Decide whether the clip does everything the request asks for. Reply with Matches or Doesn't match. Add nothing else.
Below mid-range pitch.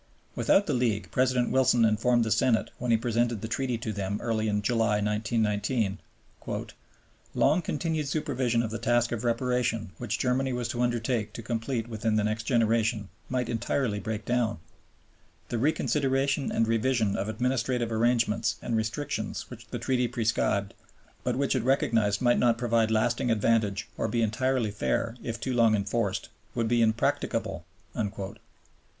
Matches